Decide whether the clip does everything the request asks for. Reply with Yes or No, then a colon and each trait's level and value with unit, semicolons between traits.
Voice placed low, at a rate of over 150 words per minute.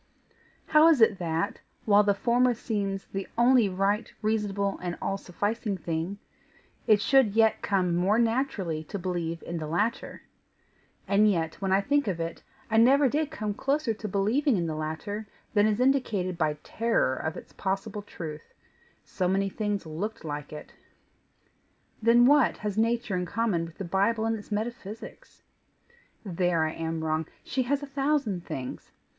No: high, 205 Hz; average, 165 wpm